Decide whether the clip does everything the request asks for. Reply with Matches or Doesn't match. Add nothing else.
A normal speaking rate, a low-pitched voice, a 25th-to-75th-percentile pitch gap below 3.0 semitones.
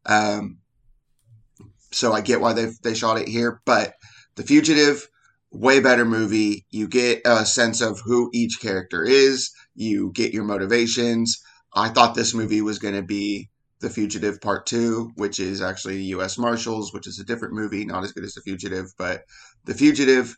Matches